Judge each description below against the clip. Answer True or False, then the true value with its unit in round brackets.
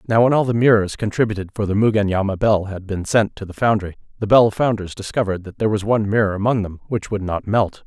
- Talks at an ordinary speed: False (235 wpm)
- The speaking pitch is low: True (105 Hz)